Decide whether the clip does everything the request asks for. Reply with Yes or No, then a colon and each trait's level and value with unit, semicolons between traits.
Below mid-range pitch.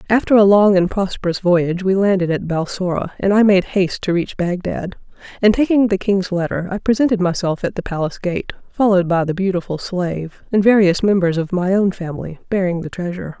No: medium, 185 Hz